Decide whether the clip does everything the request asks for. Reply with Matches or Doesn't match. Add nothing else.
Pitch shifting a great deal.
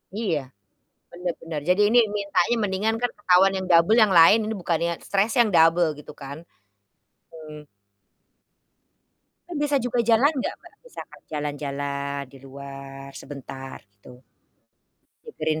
Matches